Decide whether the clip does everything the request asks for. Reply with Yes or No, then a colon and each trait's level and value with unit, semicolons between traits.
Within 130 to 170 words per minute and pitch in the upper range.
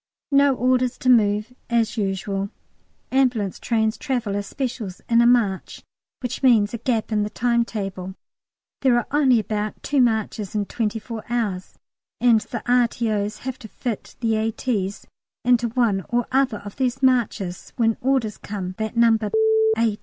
Yes: average, 160 wpm; high, 230 Hz